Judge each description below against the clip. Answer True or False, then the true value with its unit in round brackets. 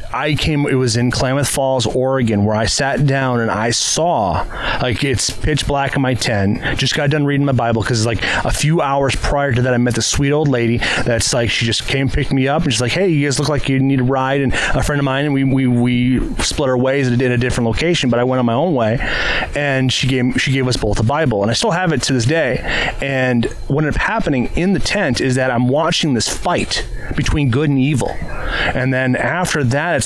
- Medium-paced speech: False (255 wpm)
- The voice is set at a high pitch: False (130 Hz)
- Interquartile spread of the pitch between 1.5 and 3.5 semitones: True (2.5 semitones)